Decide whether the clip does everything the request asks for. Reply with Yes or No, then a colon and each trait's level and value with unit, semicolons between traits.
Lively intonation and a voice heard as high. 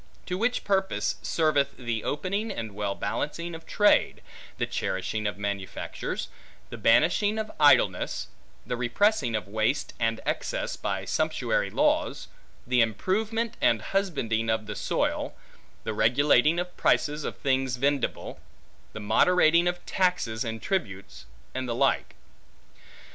No: wide, 8.2 semitones; low, 135 Hz